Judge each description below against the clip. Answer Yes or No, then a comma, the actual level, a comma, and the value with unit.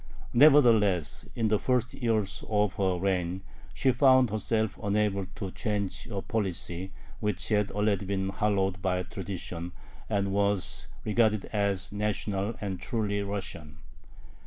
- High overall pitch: No, low, 100 Hz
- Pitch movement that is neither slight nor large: No, narrow, 2.1 semitones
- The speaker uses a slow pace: Yes, slow, 130 wpm